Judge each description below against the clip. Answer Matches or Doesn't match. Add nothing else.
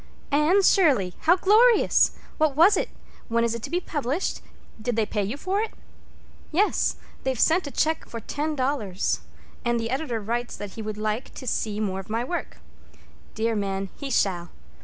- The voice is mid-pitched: Doesn't match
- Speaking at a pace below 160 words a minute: Doesn't match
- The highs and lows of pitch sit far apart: Matches